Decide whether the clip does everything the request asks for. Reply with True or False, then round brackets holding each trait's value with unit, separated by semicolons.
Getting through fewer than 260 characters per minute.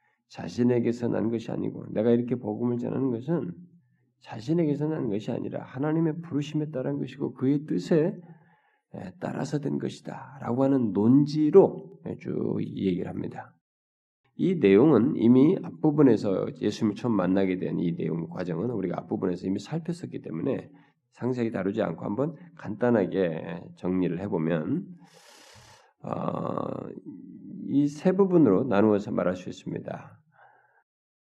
False (300 characters per minute)